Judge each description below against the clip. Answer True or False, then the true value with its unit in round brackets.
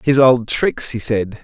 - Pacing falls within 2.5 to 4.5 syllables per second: True (3.8 syllables/s)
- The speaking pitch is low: True (120 Hz)